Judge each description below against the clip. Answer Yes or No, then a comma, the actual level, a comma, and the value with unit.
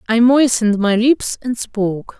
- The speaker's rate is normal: Yes, average, 165 wpm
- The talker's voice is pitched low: No, high, 230 Hz